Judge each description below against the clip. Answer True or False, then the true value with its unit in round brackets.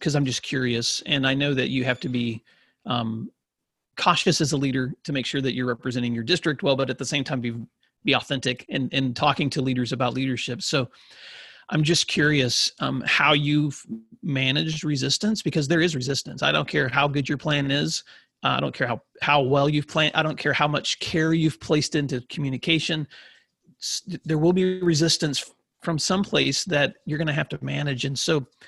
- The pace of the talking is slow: False (200 wpm)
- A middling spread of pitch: True (3.2 semitones)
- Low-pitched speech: False (145 Hz)